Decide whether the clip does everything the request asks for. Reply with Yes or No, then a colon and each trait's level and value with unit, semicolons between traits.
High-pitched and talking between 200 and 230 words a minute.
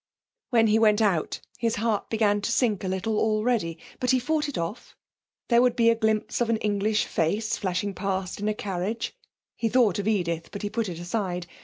Yes: high, 215 Hz; fast, 205 wpm